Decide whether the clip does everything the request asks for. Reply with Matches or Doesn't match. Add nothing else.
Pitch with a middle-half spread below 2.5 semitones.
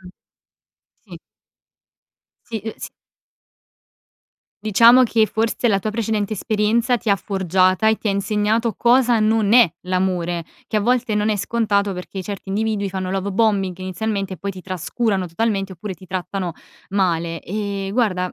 Doesn't match